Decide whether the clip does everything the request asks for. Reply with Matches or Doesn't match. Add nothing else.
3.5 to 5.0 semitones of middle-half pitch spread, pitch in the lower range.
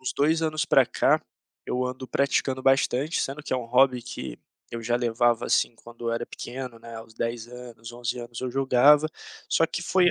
Doesn't match